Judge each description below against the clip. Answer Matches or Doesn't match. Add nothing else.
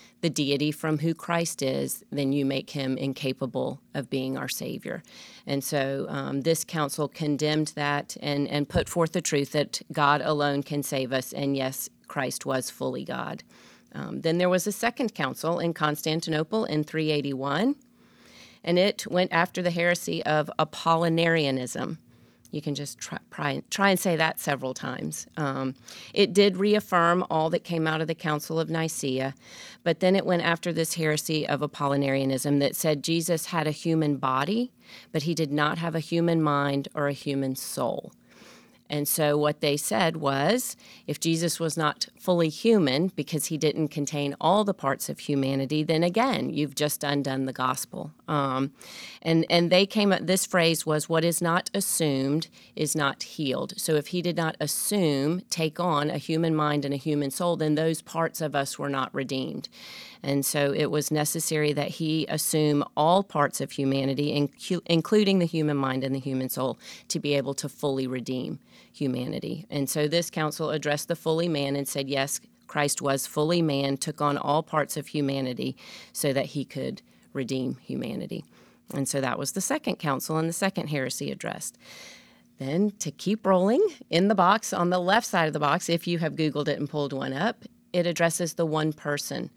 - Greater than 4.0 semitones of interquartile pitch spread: Doesn't match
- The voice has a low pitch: Doesn't match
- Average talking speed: Matches